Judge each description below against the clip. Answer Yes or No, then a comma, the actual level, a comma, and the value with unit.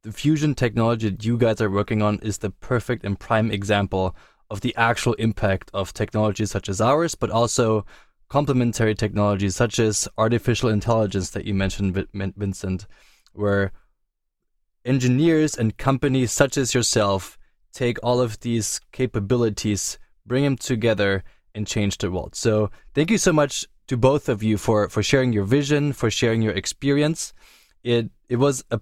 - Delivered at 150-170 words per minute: Yes, average, 160 wpm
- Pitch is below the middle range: Yes, low, 110 Hz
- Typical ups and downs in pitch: Yes, average, 3.5 semitones